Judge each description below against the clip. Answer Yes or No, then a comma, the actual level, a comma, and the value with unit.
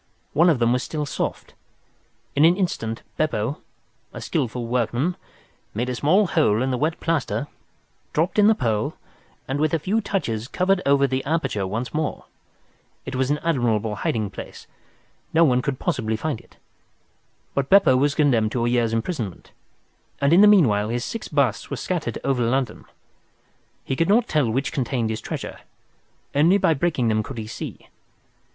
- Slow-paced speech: No, average, 170 wpm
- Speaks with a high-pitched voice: No, low, 135 Hz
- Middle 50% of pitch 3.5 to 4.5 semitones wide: No, wide, 5.5 semitones